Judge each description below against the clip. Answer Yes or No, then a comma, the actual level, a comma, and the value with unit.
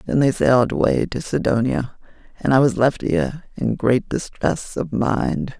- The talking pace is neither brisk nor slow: Yes, average, 170 wpm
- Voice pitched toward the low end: Yes, low, 130 Hz